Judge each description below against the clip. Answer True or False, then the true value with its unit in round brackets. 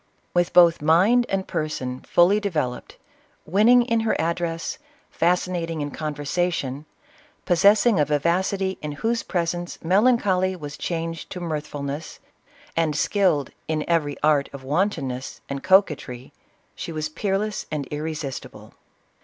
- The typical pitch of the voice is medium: True (165 Hz)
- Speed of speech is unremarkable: False (130 wpm)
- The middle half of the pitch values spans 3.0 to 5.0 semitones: True (4.2 semitones)